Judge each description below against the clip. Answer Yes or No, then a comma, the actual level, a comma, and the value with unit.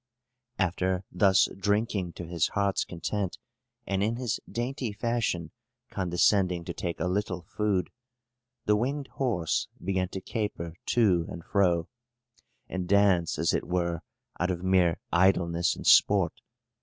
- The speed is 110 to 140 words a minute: Yes, slow, 135 wpm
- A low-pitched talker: Yes, very low, 95 Hz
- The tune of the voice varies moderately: Yes, average, 3.0 semitones